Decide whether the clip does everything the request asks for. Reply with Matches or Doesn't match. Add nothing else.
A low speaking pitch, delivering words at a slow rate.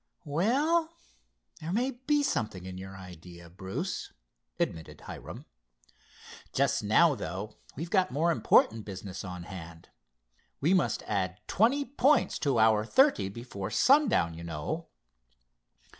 Matches